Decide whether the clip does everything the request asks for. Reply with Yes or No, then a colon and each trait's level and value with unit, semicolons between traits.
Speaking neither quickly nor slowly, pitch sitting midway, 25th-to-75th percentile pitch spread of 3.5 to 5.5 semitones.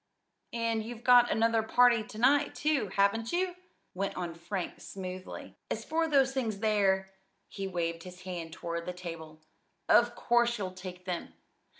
No: average, 160 wpm; high, 200 Hz; average, 4.8 semitones